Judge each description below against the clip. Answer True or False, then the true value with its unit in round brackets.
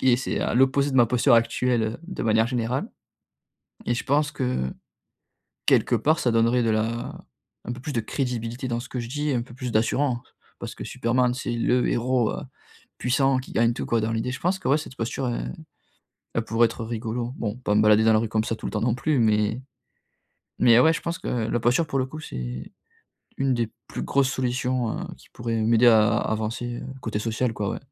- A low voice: True (120 Hz)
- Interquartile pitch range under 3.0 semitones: True (2.4 semitones)